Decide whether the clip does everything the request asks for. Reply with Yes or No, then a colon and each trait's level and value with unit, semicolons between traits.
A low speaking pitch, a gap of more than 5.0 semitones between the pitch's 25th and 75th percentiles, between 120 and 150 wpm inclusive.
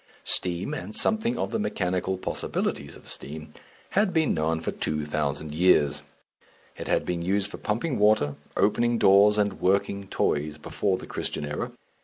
No: very low, 95 Hz; wide, 5.4 semitones; average, 160 wpm